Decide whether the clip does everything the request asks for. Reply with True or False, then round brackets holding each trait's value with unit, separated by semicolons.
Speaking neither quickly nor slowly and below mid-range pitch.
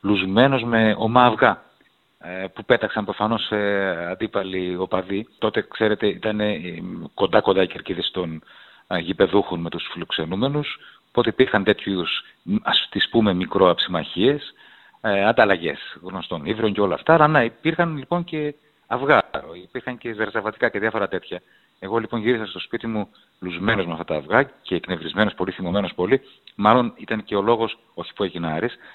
True (145 wpm; 110 Hz)